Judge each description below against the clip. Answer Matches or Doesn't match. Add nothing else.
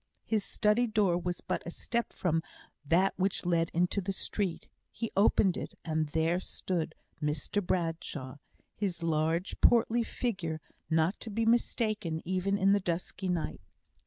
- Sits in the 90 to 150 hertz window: Doesn't match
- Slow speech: Doesn't match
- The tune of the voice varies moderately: Matches